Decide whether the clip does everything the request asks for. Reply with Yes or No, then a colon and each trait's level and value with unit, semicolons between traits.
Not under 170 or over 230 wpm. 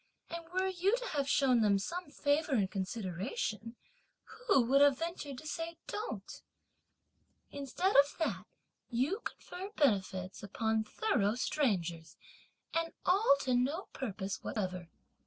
No: slow, 135 wpm